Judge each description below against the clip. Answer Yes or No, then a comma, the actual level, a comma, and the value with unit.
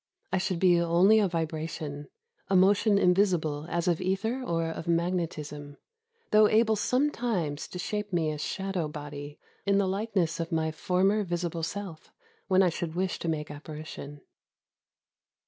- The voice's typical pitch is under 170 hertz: No, medium, 175 Hz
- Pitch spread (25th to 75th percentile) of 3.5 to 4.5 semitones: Yes, average, 3.8 semitones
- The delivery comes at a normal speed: Yes, average, 155 wpm